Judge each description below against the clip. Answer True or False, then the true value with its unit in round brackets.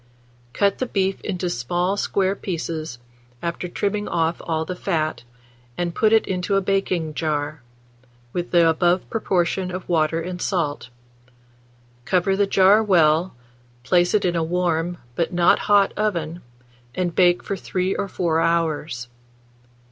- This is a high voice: False (175 Hz)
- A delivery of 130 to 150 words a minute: True (145 wpm)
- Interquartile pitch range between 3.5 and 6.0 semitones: False (2.8 semitones)